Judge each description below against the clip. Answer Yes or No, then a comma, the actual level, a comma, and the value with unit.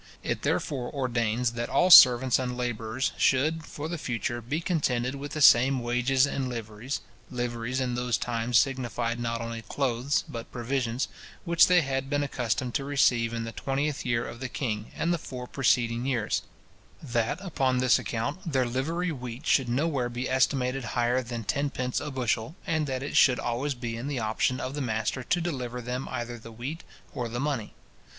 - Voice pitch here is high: No, low, 125 Hz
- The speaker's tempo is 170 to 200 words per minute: Yes, average, 185 wpm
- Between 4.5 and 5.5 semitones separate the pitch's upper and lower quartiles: No, narrow, 2.6 semitones